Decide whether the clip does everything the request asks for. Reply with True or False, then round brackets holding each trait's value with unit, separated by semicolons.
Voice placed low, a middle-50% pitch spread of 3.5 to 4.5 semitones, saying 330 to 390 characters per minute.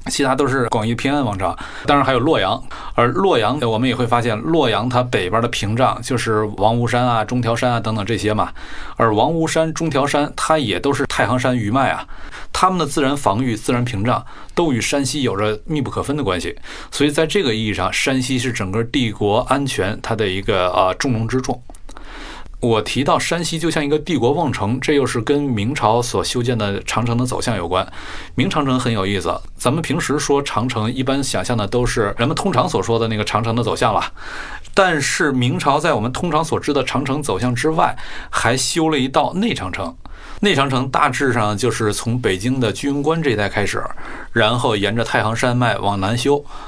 False (125 Hz; 4.0 semitones; 305 characters per minute)